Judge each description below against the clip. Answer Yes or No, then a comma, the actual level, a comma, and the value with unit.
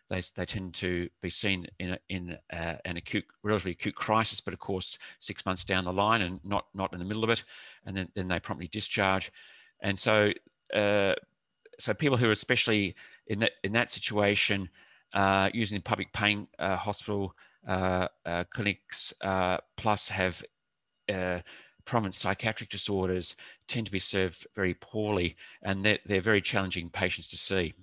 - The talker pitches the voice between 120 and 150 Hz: No, very low, 95 Hz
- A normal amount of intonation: No, narrow, 2.3 semitones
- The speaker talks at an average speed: Yes, average, 170 wpm